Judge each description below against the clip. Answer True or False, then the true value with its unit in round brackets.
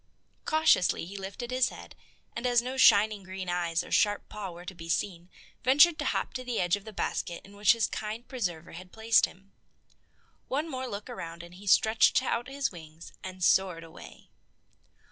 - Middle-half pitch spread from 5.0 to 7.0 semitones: True (5.3 semitones)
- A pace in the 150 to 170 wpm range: False (190 wpm)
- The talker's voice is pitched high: True (200 Hz)